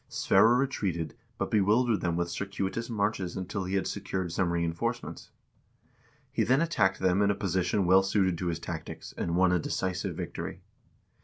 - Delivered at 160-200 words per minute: Yes, average, 165 wpm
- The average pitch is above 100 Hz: No, very low, 95 Hz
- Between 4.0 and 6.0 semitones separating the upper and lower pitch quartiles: No, average, 2.8 semitones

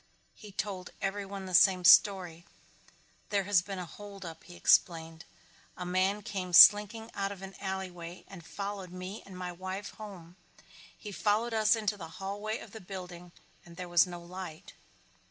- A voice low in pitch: No, high, 190 Hz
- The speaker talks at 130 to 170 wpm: Yes, average, 165 wpm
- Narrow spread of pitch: Yes, narrow, 2.3 semitones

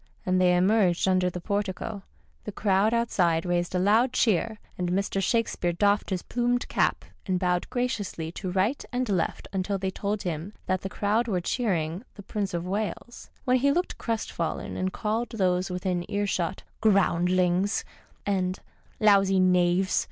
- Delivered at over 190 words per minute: No, average, 165 wpm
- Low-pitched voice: No, high, 190 Hz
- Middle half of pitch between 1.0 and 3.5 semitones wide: Yes, average, 2.9 semitones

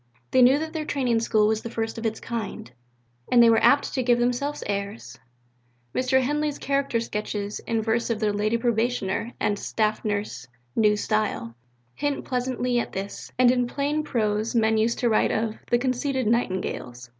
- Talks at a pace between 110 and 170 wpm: No, average, 180 wpm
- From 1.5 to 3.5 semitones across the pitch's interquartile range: Yes, average, 2.9 semitones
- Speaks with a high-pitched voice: Yes, high, 230 Hz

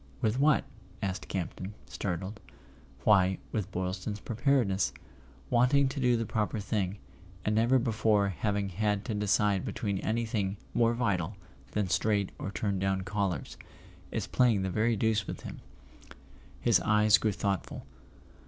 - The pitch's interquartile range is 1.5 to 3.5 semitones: Yes, average, 2.7 semitones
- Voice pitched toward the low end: Yes, low, 105 Hz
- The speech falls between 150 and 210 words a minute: No, slow, 135 wpm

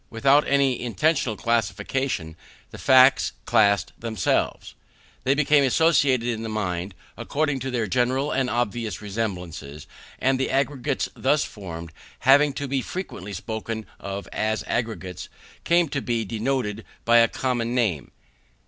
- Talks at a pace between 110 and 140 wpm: Yes, slow, 135 wpm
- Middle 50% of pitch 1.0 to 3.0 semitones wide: No, average, 4.5 semitones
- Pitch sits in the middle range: No, low, 120 Hz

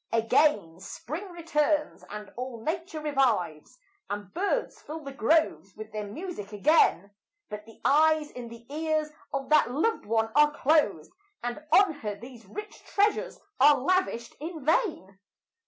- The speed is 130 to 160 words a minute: Yes, average, 145 wpm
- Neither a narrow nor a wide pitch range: No, wide, 6.6 semitones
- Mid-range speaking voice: No, very high, 280 Hz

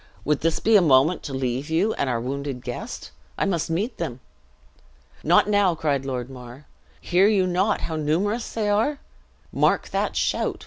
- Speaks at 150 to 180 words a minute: Yes, average, 175 wpm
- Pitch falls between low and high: Yes, medium, 160 Hz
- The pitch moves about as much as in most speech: No, wide, 6.8 semitones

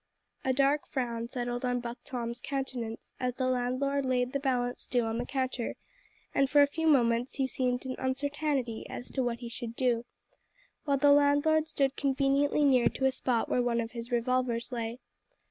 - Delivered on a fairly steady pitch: Yes, narrow, 2.3 semitones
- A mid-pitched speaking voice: No, very high, 255 Hz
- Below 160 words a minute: No, average, 185 wpm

